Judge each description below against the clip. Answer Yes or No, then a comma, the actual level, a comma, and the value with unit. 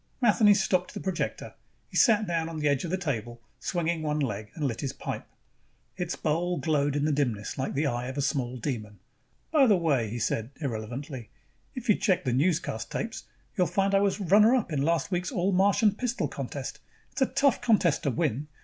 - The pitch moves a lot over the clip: Yes, wide, 6.6 semitones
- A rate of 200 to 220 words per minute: Yes, fast, 205 wpm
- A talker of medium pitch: Yes, medium, 160 Hz